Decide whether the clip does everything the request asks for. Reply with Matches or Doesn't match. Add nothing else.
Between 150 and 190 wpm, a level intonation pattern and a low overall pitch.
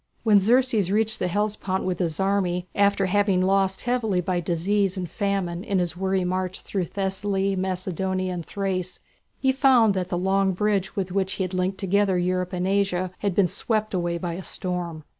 Doesn't match